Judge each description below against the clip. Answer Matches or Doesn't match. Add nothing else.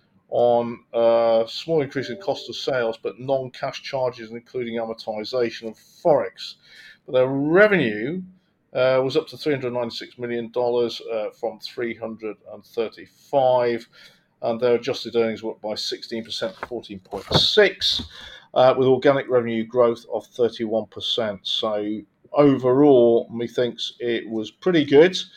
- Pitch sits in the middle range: Doesn't match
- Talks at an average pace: Doesn't match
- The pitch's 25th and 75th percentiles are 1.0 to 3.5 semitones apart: Matches